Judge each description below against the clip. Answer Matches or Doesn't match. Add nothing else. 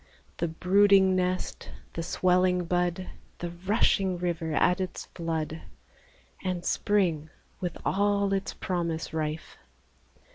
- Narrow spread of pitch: Matches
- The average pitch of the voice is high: Doesn't match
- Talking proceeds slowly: Matches